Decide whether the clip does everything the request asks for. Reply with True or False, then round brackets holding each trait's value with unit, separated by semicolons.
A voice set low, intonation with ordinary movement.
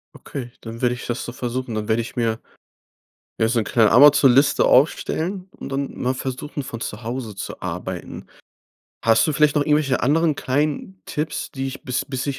True (130 Hz; 3.9 semitones)